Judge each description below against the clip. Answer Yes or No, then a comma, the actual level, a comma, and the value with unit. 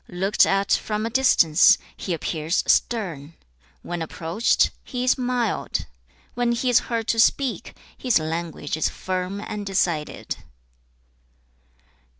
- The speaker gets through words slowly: Yes, slow, 125 wpm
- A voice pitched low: No, high, 195 Hz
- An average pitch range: No, wide, 5.9 semitones